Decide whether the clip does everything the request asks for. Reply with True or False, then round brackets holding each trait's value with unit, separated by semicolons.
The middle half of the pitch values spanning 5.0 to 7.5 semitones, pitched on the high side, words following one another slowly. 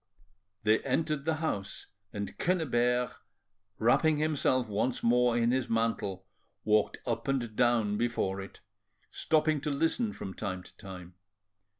False (5.4 semitones; 120 Hz; 130 wpm)